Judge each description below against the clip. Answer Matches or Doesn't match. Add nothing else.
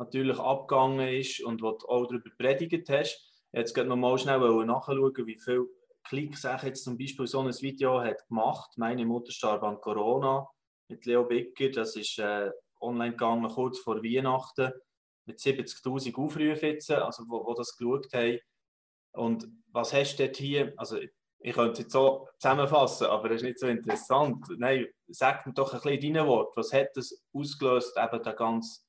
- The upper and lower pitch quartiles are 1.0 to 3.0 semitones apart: Matches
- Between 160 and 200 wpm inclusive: Matches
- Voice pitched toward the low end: Matches